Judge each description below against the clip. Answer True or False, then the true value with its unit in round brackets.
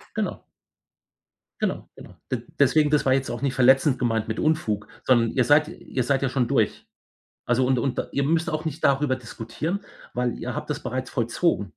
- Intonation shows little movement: False (3.3 semitones)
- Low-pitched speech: True (130 Hz)